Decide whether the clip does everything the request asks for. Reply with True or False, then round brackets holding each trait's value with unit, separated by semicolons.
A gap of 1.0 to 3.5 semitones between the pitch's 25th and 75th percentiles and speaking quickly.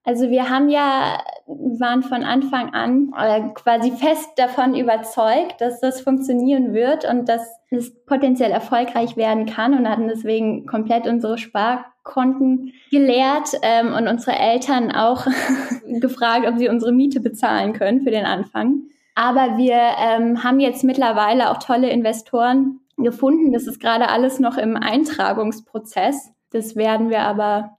False (2.5 semitones; 145 wpm)